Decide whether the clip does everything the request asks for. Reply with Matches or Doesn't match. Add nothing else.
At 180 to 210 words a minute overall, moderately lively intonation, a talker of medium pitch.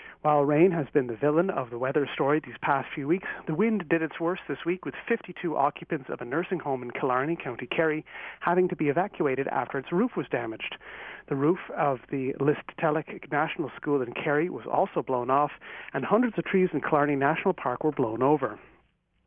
Matches